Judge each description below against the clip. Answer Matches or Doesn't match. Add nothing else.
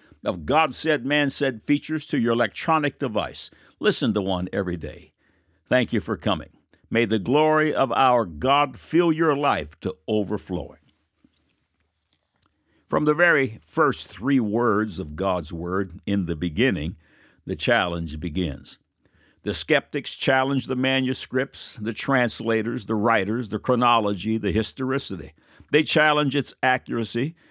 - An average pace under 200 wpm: Matches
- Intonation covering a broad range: Matches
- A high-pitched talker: Doesn't match